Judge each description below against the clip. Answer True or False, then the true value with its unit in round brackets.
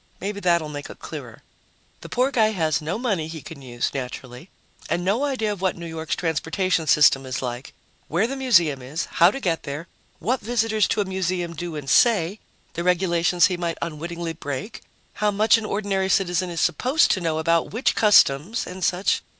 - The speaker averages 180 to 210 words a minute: True (190 wpm)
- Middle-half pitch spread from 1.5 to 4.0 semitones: False (4.4 semitones)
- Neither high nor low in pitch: True (175 Hz)